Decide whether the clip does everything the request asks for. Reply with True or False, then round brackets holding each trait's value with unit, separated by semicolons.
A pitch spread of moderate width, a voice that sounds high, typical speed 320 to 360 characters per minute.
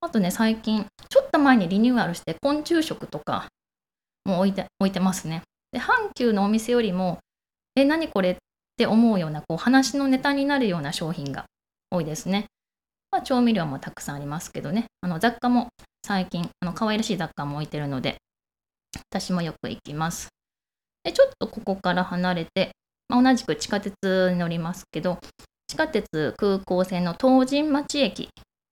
False (5.7 semitones; 200 Hz; 330 characters per minute)